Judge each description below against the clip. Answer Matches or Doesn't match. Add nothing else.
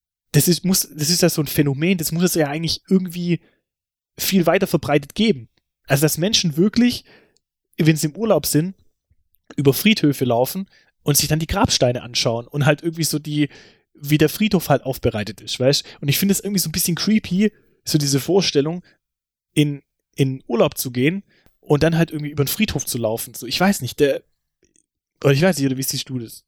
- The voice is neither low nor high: Matches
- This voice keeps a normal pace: Doesn't match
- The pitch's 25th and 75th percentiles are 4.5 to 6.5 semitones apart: Matches